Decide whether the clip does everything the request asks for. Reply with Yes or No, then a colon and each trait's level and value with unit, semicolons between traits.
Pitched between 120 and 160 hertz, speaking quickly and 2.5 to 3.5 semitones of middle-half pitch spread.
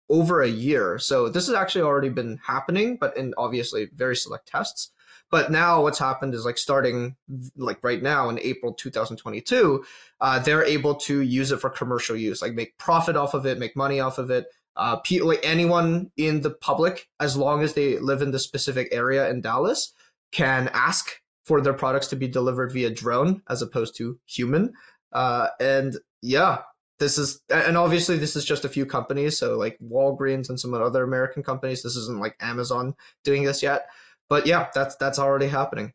No: low, 135 Hz; average, 190 wpm; average, 2.8 semitones